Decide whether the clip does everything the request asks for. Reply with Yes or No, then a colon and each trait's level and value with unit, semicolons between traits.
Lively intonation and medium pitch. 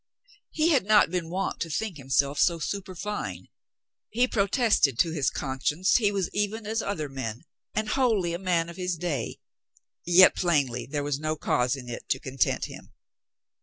Yes: wide, 6.4 semitones; medium, 170 Hz